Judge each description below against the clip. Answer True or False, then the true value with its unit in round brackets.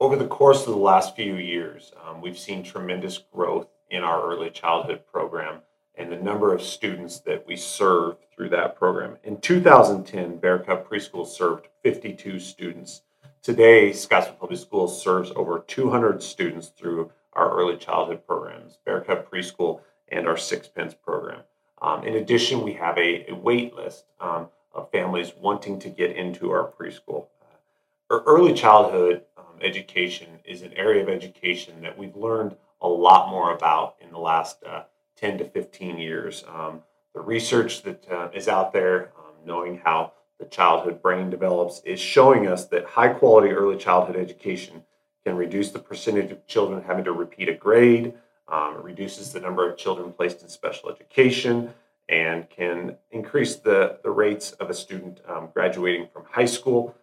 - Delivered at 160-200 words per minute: True (165 wpm)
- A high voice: False (100 Hz)